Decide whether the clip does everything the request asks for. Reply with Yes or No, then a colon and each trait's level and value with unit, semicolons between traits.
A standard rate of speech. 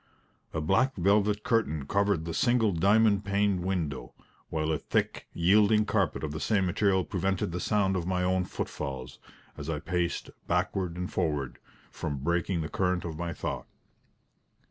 Yes: average, 160 wpm